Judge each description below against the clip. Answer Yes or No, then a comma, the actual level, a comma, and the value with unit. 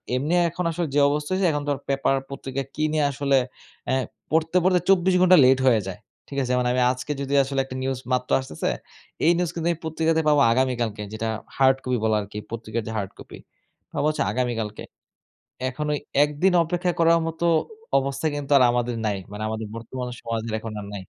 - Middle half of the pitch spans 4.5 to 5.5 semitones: Yes, average, 5.2 semitones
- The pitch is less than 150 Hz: Yes, low, 135 Hz